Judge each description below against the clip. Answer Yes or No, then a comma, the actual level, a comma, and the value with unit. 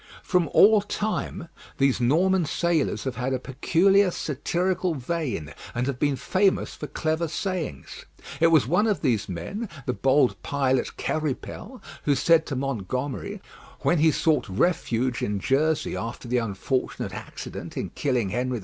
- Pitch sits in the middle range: Yes, medium, 145 Hz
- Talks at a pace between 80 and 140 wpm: No, average, 150 wpm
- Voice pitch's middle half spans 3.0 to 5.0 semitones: No, wide, 5.5 semitones